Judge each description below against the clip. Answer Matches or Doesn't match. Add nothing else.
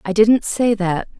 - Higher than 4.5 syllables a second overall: Doesn't match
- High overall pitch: Matches